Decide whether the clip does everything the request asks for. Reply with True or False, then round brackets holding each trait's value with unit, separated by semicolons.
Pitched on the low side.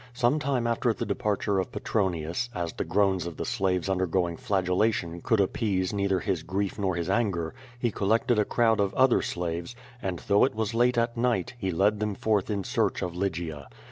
True (100 Hz)